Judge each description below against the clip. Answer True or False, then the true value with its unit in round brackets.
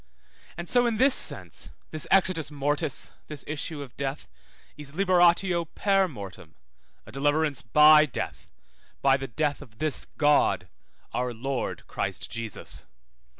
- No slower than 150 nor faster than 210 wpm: False (135 wpm)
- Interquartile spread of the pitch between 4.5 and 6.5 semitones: False (4.0 semitones)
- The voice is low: False (150 Hz)